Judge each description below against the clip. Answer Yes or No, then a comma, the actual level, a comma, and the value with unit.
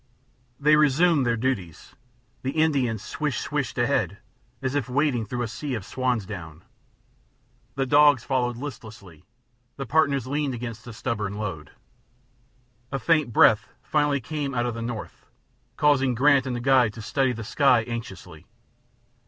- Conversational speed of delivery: Yes, average, 150 wpm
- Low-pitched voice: Yes, low, 125 Hz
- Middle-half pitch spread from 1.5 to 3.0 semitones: No, average, 4.0 semitones